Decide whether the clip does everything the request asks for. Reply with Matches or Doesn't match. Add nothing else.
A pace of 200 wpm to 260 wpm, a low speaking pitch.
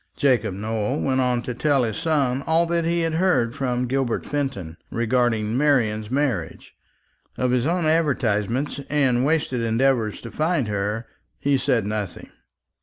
Doesn't match